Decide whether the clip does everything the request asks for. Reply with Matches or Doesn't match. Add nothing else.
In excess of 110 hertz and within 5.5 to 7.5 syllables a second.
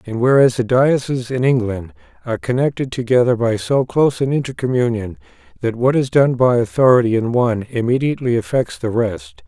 Matches